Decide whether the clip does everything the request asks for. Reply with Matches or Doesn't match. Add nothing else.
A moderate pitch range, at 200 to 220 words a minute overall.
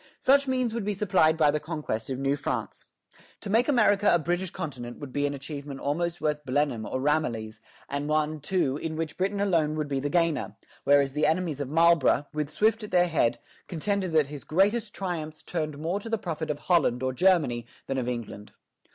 Matches